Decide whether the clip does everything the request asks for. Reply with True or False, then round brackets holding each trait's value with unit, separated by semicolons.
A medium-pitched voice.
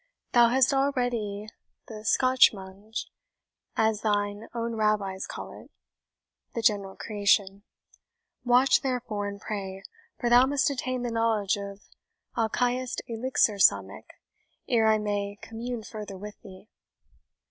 False (220 Hz)